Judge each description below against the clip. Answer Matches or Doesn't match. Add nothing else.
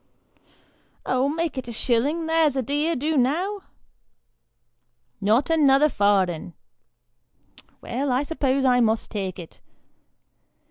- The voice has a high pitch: Matches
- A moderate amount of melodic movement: Matches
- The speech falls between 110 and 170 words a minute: Matches